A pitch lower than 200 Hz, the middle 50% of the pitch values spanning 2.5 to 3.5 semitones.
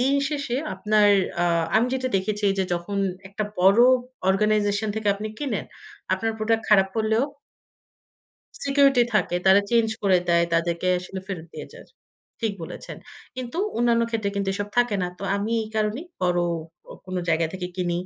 No: high, 210 Hz; average, 3.2 semitones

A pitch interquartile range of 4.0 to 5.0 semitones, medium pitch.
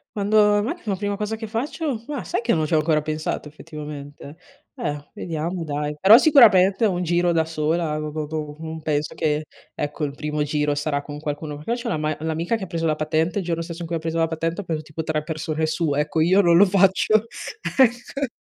Yes: average, 4.3 semitones; medium, 160 Hz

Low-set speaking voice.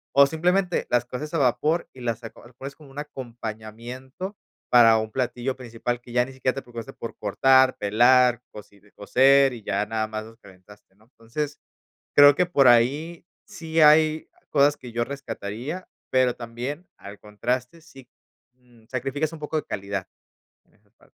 Yes: low, 125 Hz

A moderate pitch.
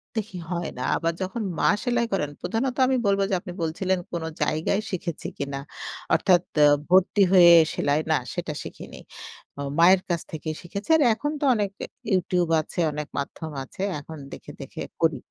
Yes: medium, 175 Hz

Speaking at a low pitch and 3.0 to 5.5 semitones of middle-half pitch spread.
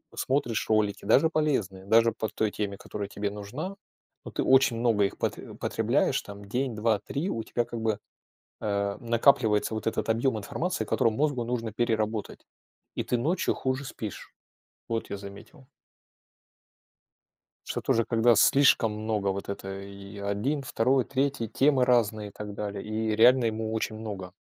Yes: low, 110 Hz; average, 3.5 semitones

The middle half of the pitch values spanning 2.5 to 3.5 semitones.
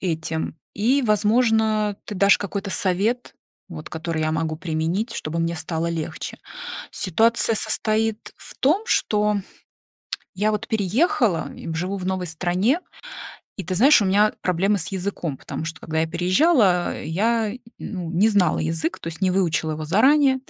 No: average, 4.7 semitones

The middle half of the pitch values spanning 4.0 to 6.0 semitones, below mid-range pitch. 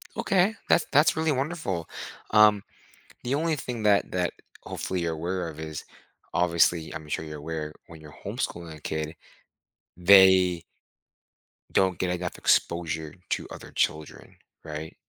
Yes: average, 4.8 semitones; very low, 90 Hz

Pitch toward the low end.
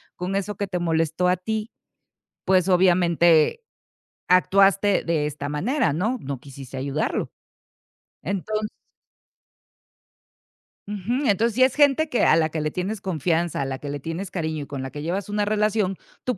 No: medium, 180 Hz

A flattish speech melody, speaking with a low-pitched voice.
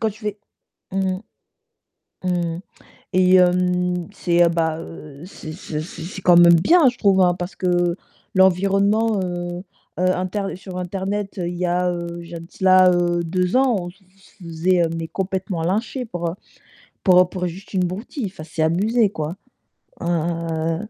No: narrow, 2.0 semitones; medium, 180 Hz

